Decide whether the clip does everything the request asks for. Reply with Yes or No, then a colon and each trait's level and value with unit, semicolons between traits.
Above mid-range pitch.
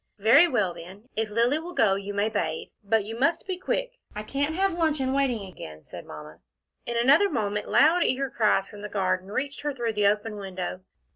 Yes: high, 225 Hz